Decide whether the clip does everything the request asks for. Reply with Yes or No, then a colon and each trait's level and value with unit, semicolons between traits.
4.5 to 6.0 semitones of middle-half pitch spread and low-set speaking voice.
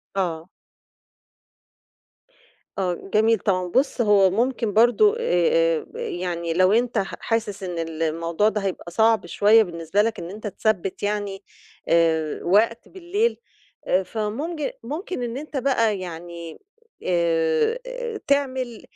No: average, 5.1 semitones; high, 205 Hz